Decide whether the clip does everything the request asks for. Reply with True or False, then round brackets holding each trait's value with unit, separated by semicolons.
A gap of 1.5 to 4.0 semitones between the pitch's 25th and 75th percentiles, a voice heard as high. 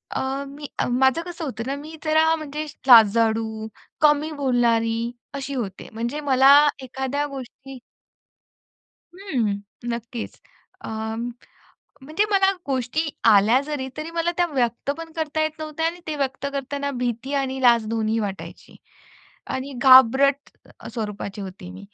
False (4.5 semitones; 265 Hz)